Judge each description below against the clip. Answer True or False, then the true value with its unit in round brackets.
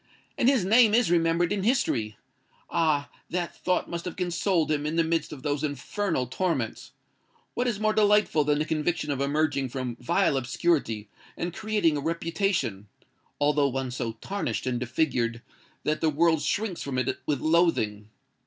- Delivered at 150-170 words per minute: True (165 wpm)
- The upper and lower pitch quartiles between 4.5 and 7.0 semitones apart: True (5.0 semitones)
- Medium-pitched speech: True (155 Hz)